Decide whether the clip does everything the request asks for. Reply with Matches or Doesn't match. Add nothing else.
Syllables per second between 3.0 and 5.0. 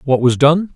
Matches